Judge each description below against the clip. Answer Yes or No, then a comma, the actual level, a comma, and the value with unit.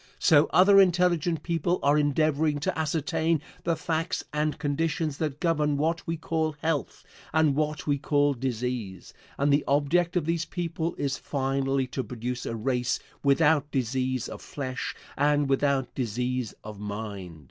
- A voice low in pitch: No, medium, 145 Hz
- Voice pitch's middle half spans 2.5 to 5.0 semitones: Yes, average, 3.6 semitones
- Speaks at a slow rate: No, average, 150 wpm